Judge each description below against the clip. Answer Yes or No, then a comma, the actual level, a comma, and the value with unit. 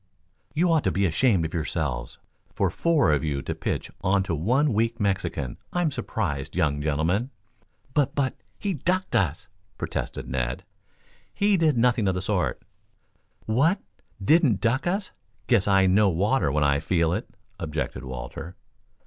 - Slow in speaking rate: No, average, 155 wpm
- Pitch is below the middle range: Yes, low, 100 Hz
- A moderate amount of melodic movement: No, wide, 8.8 semitones